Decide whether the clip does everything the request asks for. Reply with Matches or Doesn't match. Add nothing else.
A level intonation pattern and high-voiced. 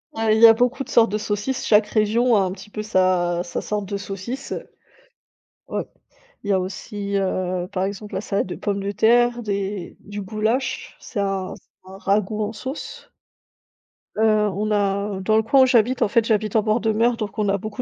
Matches